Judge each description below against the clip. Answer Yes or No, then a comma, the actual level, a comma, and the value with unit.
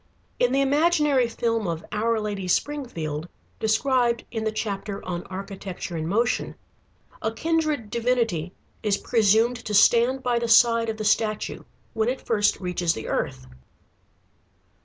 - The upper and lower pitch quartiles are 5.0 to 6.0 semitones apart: No, average, 3.6 semitones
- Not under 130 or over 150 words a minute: Yes, average, 140 wpm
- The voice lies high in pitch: Yes, high, 225 Hz